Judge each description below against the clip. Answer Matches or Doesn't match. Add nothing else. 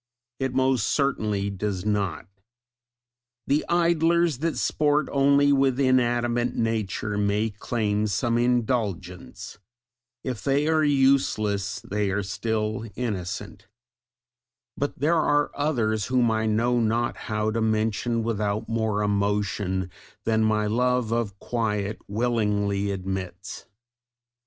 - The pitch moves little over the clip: Doesn't match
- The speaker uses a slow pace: Matches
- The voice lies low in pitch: Matches